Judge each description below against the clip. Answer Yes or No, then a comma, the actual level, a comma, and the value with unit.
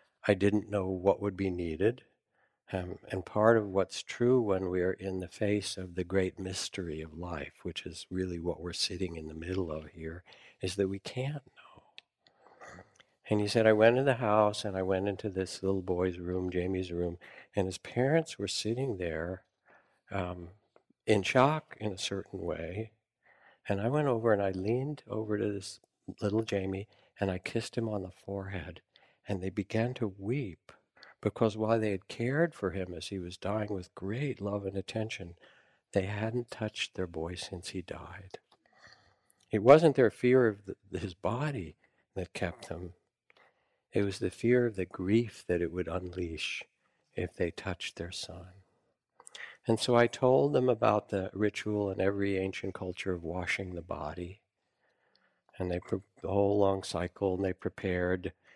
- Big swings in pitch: No, average, 3.0 semitones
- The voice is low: Yes, very low, 95 Hz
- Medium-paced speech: Yes, average, 175 wpm